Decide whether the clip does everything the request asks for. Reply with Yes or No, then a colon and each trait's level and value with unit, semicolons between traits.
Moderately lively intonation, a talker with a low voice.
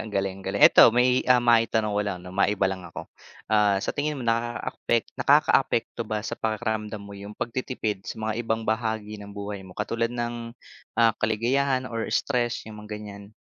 No: narrow, 2.3 semitones; low, 110 Hz